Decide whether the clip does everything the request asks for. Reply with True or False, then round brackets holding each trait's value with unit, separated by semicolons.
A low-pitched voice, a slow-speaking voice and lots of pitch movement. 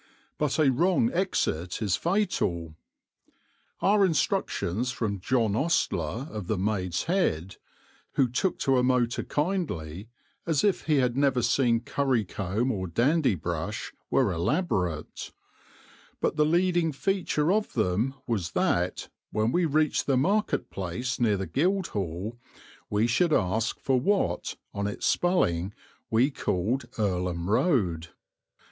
True (120 Hz; 130 wpm; 8.5 semitones)